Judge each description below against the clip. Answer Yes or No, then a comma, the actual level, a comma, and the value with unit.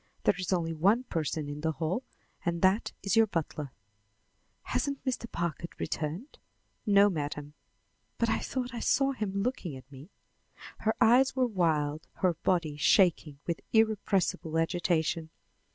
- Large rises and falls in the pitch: Yes, wide, 5.8 semitones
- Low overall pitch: No, medium, 175 Hz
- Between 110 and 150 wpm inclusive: Yes, average, 145 wpm